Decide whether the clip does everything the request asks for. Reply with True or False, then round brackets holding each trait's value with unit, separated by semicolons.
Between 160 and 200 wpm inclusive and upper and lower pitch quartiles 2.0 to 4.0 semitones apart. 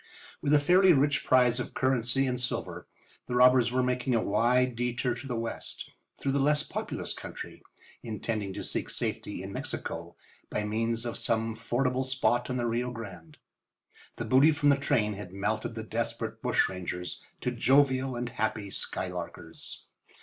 True (165 wpm; 2.8 semitones)